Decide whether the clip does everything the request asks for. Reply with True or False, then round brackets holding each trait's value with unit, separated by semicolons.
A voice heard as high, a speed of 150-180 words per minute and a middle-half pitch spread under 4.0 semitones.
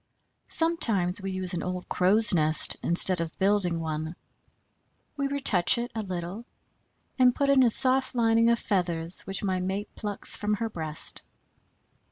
False (195 Hz; 155 wpm; 4.6 semitones)